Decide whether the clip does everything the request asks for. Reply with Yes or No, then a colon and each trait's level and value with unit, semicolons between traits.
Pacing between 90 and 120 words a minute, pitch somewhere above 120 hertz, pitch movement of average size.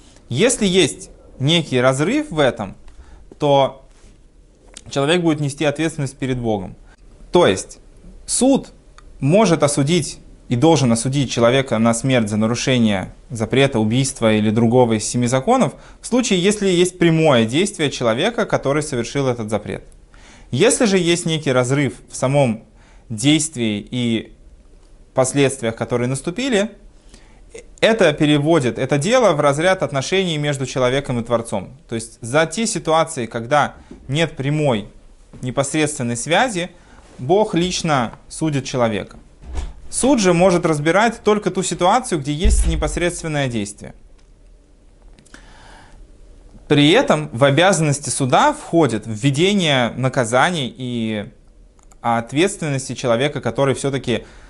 No: average, 115 wpm; medium, 140 Hz; wide, 5.9 semitones